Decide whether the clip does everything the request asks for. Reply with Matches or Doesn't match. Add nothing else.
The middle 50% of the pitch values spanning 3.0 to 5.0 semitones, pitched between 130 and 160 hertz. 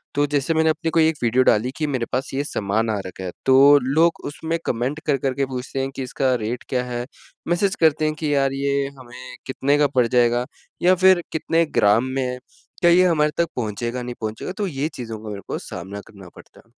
Matches